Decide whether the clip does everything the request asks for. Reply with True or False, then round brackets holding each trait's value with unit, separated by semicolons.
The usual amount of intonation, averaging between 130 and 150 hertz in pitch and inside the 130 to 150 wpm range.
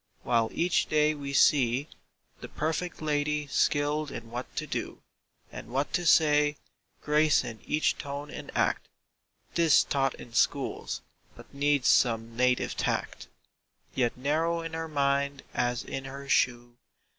True (3.1 semitones; 140 Hz; 145 wpm)